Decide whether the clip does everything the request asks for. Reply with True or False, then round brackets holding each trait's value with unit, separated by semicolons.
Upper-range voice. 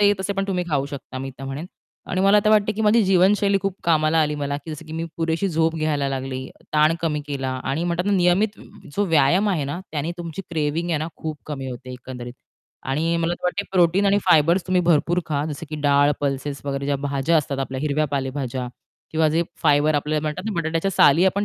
False (155 Hz)